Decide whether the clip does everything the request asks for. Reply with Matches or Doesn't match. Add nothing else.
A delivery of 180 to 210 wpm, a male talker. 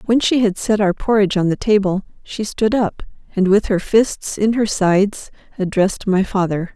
Doesn't match